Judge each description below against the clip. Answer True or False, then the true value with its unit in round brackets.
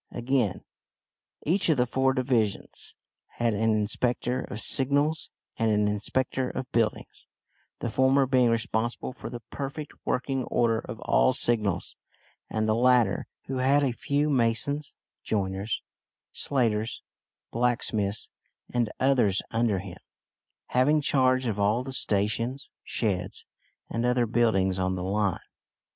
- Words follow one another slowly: True (130 wpm)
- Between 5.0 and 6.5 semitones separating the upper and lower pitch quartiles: False (3.5 semitones)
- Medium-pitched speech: False (120 Hz)